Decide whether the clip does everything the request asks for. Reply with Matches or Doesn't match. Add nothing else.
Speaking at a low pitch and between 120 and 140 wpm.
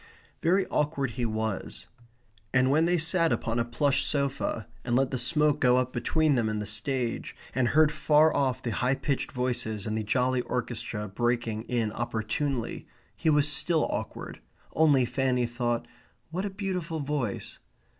Doesn't match